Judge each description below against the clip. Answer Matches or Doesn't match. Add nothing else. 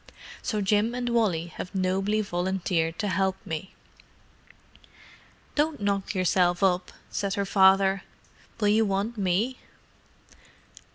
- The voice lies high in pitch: Matches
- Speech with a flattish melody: Matches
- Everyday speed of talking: Doesn't match